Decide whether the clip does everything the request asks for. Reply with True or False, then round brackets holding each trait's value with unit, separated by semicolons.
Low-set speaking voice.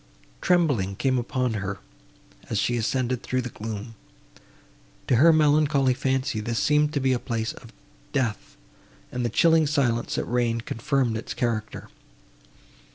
True (125 Hz)